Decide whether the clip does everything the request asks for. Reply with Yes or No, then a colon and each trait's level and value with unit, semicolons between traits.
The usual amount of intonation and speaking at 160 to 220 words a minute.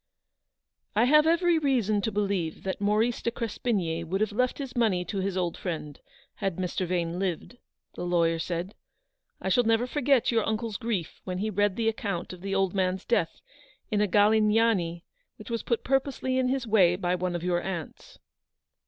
Yes: average, 4.3 semitones; average, 190 wpm